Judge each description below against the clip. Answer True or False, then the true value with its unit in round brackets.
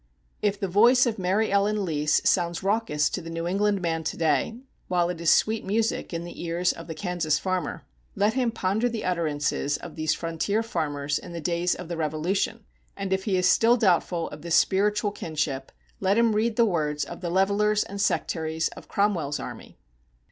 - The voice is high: False (180 Hz)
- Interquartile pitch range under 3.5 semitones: False (4.1 semitones)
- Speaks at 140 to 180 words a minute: False (195 wpm)